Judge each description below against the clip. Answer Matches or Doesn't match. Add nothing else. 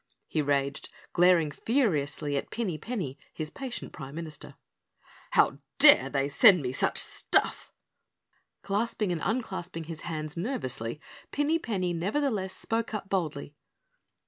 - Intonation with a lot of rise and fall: Matches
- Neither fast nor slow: Doesn't match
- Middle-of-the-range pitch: Matches